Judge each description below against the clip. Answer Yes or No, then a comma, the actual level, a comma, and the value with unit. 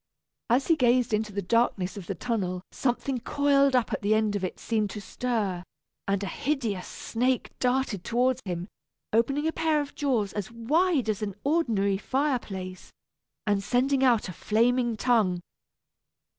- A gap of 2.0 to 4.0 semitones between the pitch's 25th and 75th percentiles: No, average, 4.6 semitones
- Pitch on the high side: Yes, high, 230 Hz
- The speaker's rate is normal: Yes, average, 160 wpm